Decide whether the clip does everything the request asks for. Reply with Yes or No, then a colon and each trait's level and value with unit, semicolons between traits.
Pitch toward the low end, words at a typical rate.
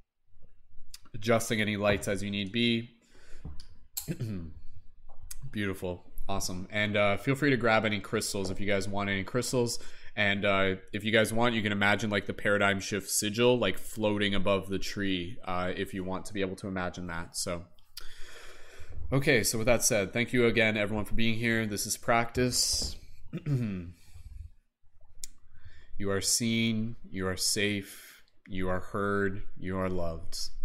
Yes: low, 100 Hz; average, 155 wpm